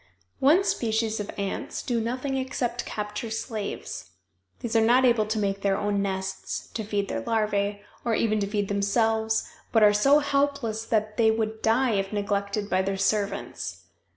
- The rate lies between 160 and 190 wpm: Yes, average, 165 wpm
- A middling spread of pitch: No, narrow, 2.3 semitones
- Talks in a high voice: Yes, high, 215 Hz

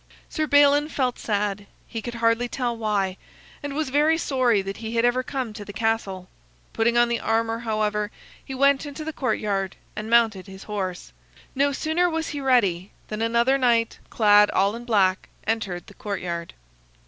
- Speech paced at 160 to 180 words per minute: Yes, average, 175 wpm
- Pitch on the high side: Yes, high, 230 Hz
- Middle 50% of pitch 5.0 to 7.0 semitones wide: No, average, 4.2 semitones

